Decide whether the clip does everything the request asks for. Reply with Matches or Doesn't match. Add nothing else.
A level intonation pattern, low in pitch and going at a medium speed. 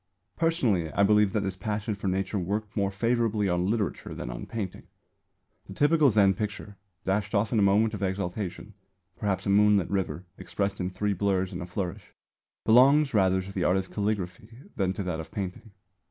Matches